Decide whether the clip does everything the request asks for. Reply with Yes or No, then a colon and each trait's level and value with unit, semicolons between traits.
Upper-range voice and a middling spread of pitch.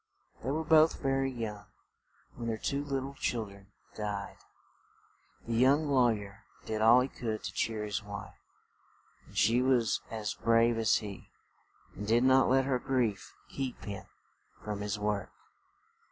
No: low, 115 Hz; average, 3.9 semitones